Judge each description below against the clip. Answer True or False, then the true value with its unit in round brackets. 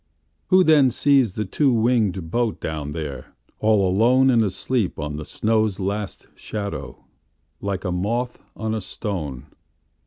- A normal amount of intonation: False (6.3 semitones)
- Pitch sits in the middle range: False (100 Hz)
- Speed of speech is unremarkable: False (125 wpm)